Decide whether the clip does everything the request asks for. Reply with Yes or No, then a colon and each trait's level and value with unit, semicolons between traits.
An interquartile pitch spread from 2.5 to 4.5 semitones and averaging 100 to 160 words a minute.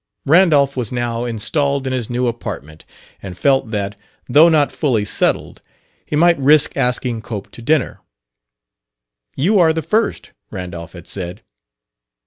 No: wide, 5.5 semitones; average, 140 wpm